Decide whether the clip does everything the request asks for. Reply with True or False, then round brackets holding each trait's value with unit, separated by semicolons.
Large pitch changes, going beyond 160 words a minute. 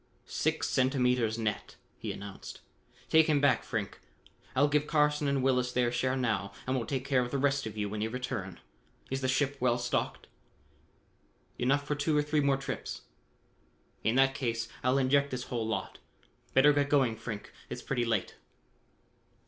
False (3.4 semitones; 175 wpm)